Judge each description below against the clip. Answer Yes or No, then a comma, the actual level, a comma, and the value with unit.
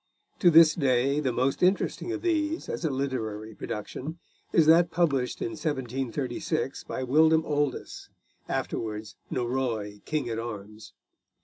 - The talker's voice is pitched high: No, low, 135 Hz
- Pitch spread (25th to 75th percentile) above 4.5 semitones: Yes, average, 5.2 semitones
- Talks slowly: Yes, slow, 130 wpm